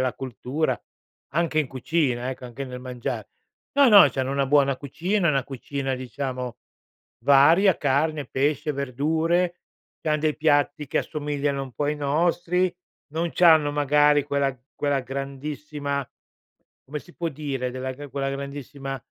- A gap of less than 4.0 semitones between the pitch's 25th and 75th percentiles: Yes, narrow, 2.4 semitones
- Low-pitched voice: No, medium, 145 Hz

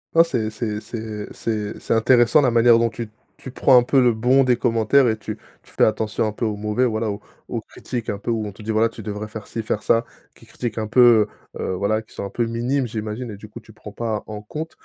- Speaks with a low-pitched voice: Yes, low, 110 Hz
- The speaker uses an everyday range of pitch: No, narrow, 2.1 semitones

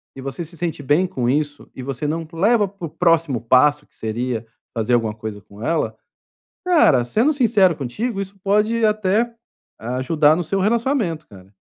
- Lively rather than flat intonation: Yes, wide, 7.8 semitones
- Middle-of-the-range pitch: Yes, medium, 160 Hz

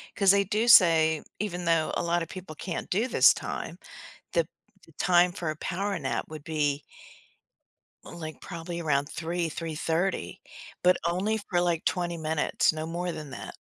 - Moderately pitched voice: Yes, medium, 170 Hz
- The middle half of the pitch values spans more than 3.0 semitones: No, narrow, 2.4 semitones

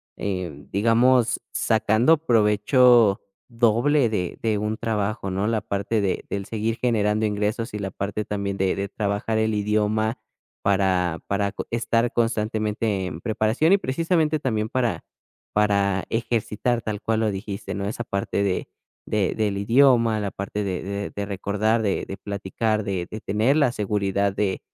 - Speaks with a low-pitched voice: Yes, low, 105 Hz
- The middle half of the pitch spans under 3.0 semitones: Yes, narrow, 2.4 semitones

